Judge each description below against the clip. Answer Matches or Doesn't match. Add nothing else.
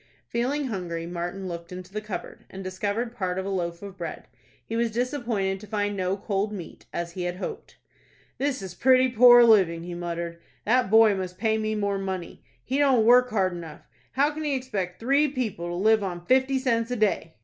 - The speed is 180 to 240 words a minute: Matches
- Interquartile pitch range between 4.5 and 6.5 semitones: Matches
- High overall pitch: Matches